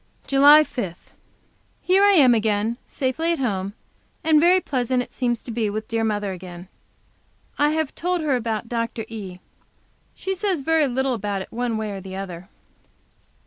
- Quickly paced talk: No, average, 170 wpm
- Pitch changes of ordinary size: No, wide, 6.2 semitones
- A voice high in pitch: Yes, high, 240 Hz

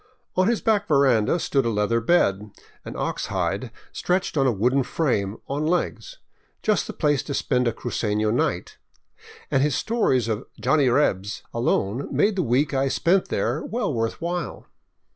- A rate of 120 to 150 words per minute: No, average, 185 wpm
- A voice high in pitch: No, low, 135 Hz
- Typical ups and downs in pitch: No, wide, 7.0 semitones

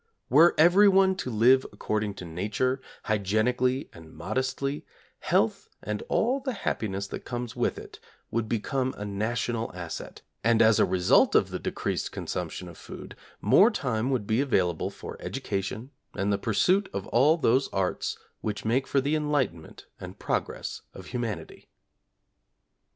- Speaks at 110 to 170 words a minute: Yes, average, 150 wpm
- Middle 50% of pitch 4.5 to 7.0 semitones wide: Yes, average, 5.1 semitones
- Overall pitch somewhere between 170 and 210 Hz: No, low, 115 Hz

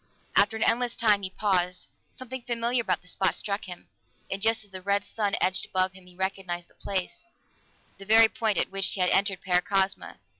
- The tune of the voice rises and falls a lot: No, average, 2.9 semitones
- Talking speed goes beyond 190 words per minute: Yes, average, 200 wpm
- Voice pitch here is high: Yes, high, 195 Hz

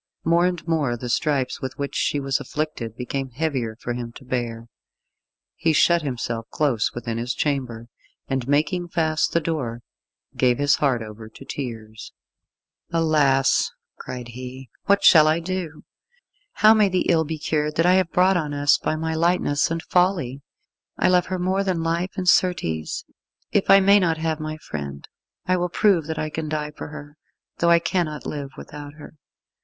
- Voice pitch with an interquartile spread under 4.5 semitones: No, average, 4.8 semitones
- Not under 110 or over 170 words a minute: No, average, 180 wpm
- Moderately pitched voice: Yes, medium, 150 Hz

